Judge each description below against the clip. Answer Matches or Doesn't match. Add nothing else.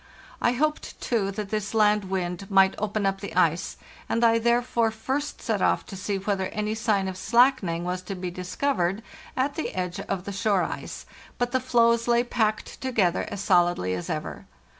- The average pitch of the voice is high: Matches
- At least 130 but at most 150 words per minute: Doesn't match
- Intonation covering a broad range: Doesn't match